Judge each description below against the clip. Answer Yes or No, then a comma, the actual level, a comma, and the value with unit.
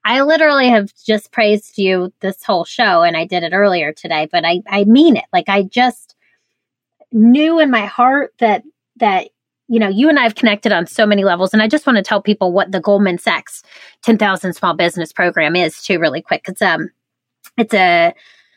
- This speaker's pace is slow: No, fast, 205 wpm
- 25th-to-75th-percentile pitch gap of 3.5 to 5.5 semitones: Yes, average, 4.7 semitones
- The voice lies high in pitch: Yes, high, 215 Hz